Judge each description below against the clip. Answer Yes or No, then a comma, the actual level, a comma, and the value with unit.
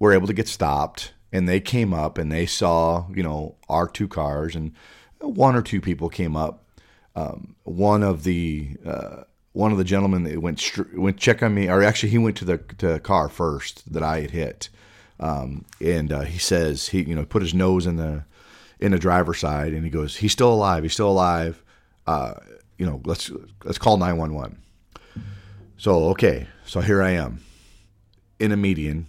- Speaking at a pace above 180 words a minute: Yes, average, 200 wpm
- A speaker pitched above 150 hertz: No, very low, 90 Hz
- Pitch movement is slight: No, average, 3.7 semitones